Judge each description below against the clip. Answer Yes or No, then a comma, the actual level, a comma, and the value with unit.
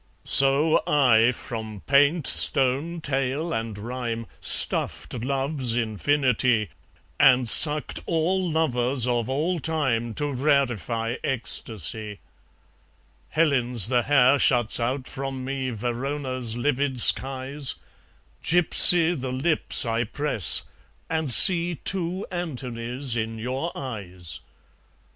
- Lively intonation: No, average, 3.8 semitones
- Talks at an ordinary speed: No, slow, 105 wpm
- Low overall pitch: Yes, low, 130 Hz